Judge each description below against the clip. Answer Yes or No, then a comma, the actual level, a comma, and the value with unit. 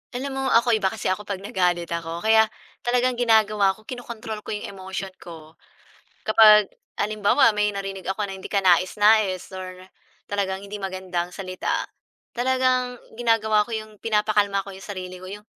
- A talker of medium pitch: No, high, 205 Hz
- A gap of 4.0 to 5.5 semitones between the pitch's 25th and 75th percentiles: No, average, 2.7 semitones